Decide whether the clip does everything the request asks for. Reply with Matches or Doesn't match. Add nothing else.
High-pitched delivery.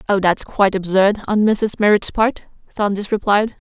Matches